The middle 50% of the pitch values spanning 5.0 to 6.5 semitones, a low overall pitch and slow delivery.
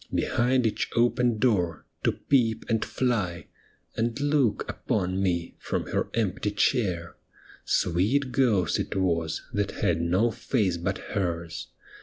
Yes: wide, 5.4 semitones; low, 105 Hz; slow, 130 wpm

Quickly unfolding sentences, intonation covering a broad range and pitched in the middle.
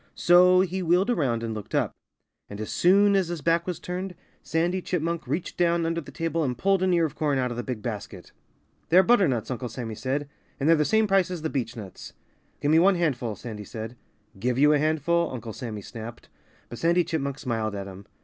Yes: fast, 215 wpm; wide, 6.7 semitones; medium, 155 Hz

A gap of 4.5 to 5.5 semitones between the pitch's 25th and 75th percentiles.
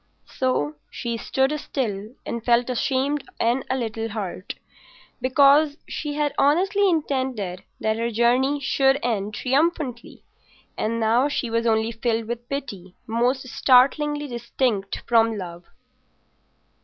No: average, 3.6 semitones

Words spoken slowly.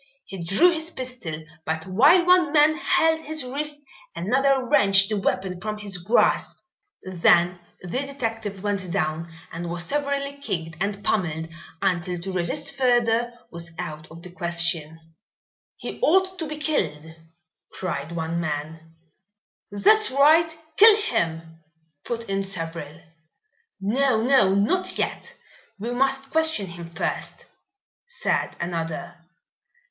Yes: slow, 130 wpm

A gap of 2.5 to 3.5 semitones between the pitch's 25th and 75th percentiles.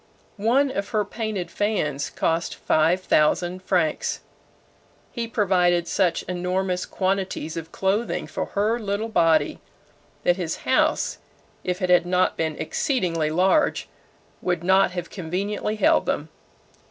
Yes: average, 3.2 semitones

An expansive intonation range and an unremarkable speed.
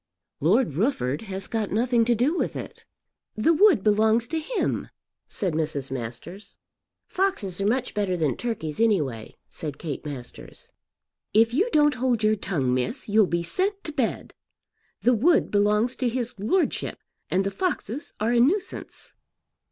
Yes: wide, 6.7 semitones; average, 155 wpm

